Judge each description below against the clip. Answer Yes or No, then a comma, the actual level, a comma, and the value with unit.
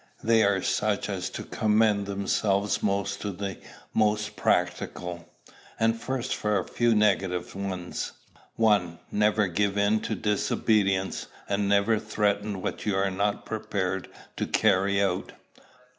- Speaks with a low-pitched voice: Yes, low, 100 Hz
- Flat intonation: Yes, narrow, 1.6 semitones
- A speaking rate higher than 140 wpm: No, slow, 135 wpm